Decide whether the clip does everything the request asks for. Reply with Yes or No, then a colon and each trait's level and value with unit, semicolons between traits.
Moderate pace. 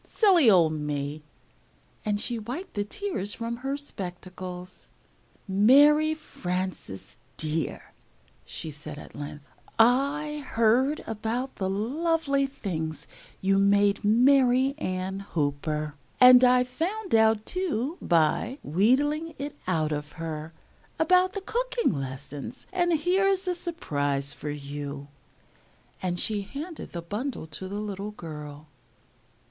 No: slow, 120 wpm